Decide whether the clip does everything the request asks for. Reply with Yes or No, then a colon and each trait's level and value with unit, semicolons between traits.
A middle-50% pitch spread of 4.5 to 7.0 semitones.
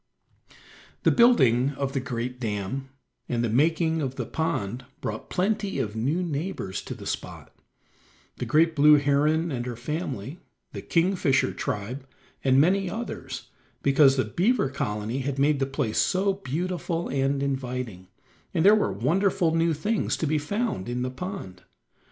Yes: average, 5.2 semitones